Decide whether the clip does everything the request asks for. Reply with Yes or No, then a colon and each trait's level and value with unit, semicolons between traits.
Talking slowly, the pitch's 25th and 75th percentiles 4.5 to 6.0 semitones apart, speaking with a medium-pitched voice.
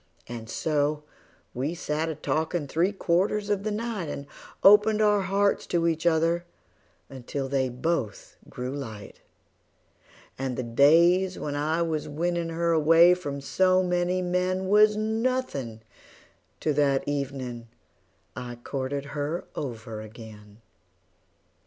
Yes: slow, 125 wpm; average, 5.2 semitones; medium, 160 Hz